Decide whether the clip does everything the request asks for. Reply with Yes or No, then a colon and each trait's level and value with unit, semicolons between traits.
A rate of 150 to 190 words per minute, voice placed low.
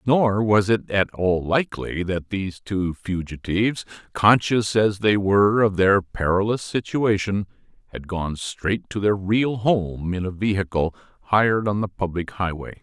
Yes: average, 155 wpm; low, 100 Hz